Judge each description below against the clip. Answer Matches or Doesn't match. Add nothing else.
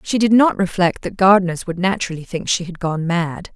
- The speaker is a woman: Matches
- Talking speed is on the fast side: Matches